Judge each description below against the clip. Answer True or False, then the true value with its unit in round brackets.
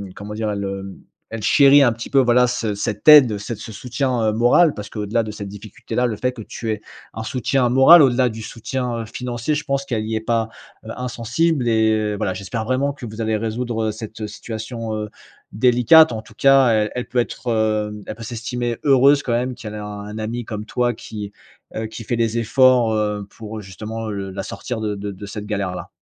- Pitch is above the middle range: False (115 Hz)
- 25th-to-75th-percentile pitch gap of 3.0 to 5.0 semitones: False (2.6 semitones)